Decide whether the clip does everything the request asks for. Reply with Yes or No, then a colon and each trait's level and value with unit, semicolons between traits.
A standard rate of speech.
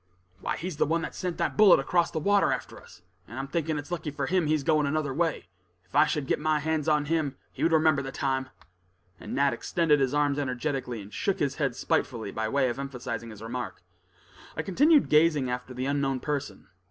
No: fast, 215 wpm